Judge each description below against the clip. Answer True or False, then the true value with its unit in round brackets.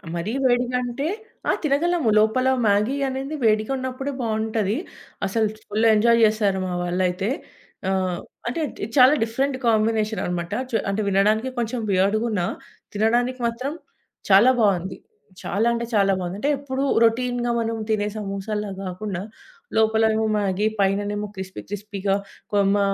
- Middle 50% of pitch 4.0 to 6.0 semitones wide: False (3.3 semitones)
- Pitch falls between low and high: False (215 Hz)